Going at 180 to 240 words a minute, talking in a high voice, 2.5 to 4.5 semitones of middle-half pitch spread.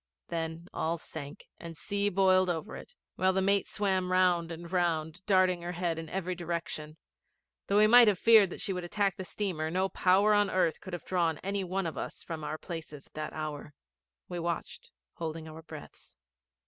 No: average, 190 wpm; medium, 175 Hz; average, 2.9 semitones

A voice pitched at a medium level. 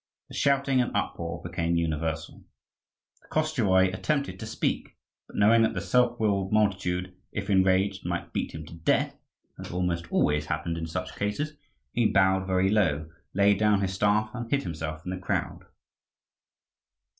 No: very low, 95 Hz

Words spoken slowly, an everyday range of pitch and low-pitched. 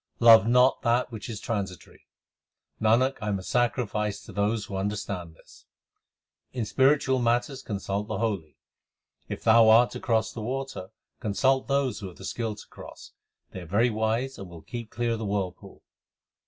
No: average, 175 wpm; average, 3.3 semitones; low, 110 Hz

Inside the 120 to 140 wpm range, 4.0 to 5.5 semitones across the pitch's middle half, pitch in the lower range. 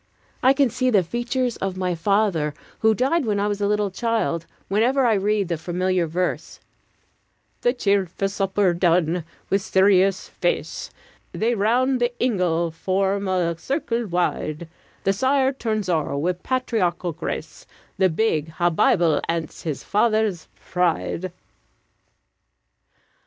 No: slow, 135 wpm; average, 4.6 semitones; high, 195 Hz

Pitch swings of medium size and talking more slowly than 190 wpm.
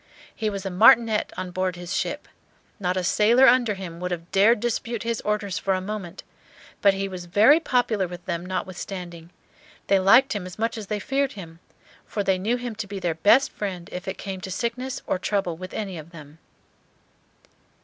No: average, 3.4 semitones; average, 200 wpm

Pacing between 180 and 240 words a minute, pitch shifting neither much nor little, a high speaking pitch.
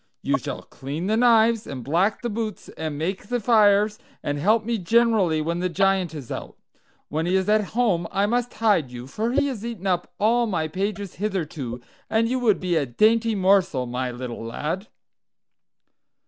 No: average, 185 wpm; wide, 5.8 semitones; high, 195 Hz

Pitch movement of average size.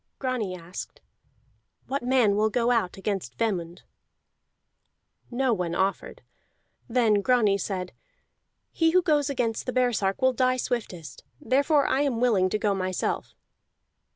Yes: average, 4.9 semitones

